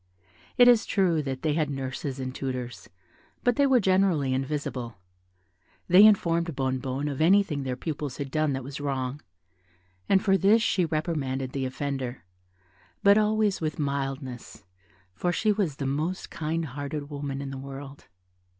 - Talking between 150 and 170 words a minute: Yes, average, 155 wpm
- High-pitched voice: No, medium, 145 Hz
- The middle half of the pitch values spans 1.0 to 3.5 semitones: No, average, 4.8 semitones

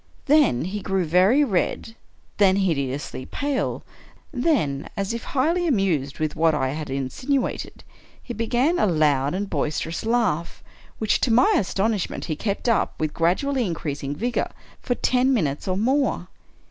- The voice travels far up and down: Yes, wide, 8.0 semitones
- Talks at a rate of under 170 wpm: Yes, average, 155 wpm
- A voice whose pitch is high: Yes, high, 195 Hz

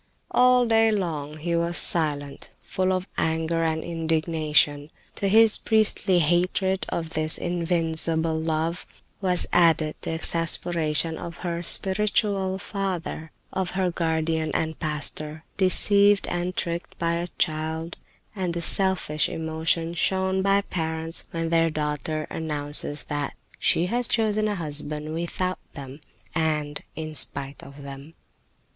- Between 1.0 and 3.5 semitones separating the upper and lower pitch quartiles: Yes, average, 2.9 semitones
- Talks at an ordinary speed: No, slow, 130 wpm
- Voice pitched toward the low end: No, medium, 165 Hz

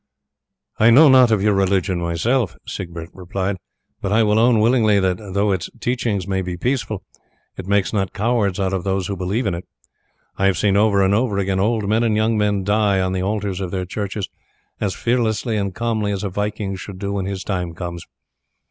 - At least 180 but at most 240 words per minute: Yes, average, 200 wpm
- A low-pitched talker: Yes, low, 100 Hz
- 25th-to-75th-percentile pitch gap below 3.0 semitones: Yes, narrow, 2.5 semitones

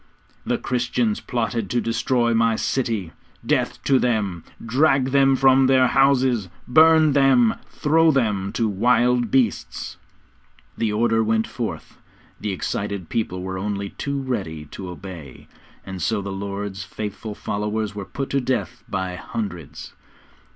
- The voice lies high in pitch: No, low, 115 Hz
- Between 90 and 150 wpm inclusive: Yes, slow, 135 wpm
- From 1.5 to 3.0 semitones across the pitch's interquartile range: No, average, 4.5 semitones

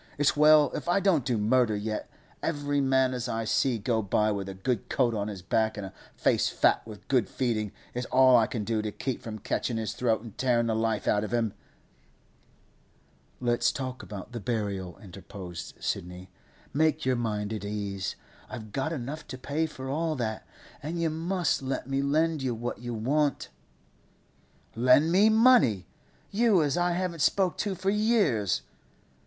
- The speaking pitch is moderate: No, low, 125 Hz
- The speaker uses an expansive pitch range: Yes, wide, 5.7 semitones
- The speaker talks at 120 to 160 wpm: No, average, 180 wpm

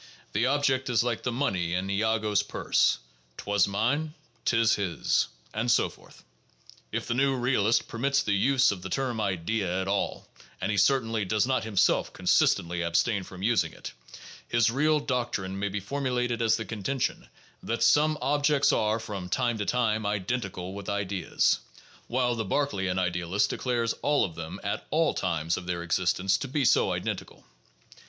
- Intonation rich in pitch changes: No, average, 4.6 semitones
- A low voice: Yes, low, 110 Hz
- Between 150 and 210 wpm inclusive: Yes, average, 175 wpm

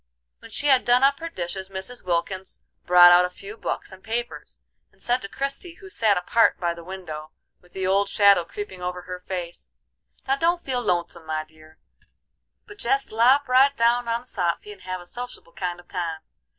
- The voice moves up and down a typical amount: No, wide, 5.7 semitones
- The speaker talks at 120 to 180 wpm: No, fast, 205 wpm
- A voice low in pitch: No, high, 190 Hz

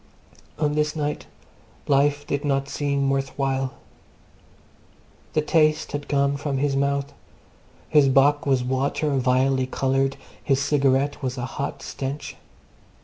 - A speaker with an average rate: No, slow, 130 wpm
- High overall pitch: No, medium, 140 Hz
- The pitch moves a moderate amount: No, narrow, 1.3 semitones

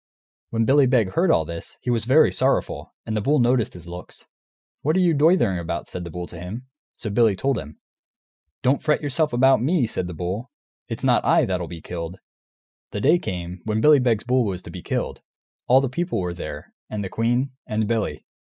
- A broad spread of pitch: Yes, wide, 6.9 semitones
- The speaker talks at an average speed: No, fast, 210 wpm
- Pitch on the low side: Yes, low, 115 Hz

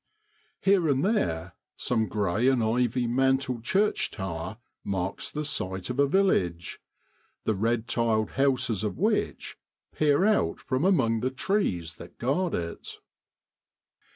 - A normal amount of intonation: No, wide, 5.9 semitones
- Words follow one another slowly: Yes, slow, 130 wpm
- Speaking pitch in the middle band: No, low, 120 Hz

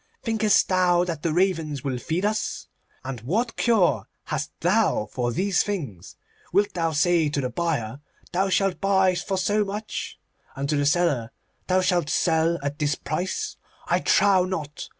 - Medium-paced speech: Yes, average, 165 wpm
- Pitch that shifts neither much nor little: Yes, average, 4.7 semitones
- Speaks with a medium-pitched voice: Yes, medium, 175 Hz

